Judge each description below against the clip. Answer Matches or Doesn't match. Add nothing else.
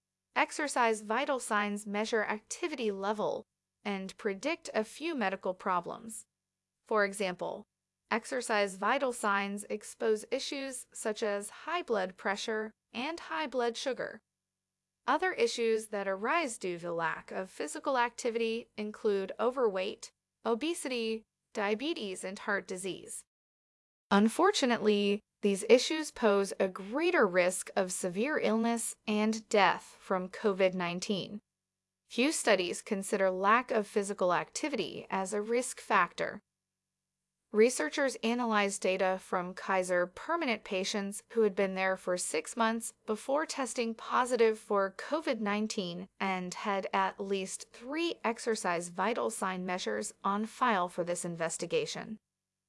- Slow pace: Matches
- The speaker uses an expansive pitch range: Doesn't match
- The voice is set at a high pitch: Matches